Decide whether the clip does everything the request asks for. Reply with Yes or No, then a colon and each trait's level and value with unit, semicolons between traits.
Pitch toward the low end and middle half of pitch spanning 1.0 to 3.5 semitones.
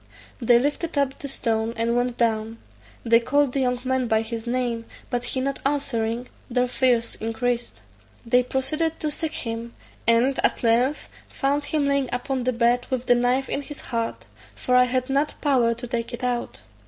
No: very high, 250 Hz; narrow, 2.6 semitones